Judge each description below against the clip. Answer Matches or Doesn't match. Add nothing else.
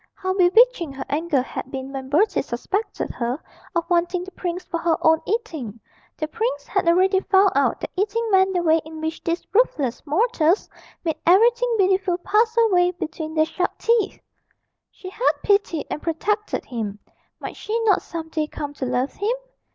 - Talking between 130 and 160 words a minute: Doesn't match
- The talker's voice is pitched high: Matches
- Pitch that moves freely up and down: Doesn't match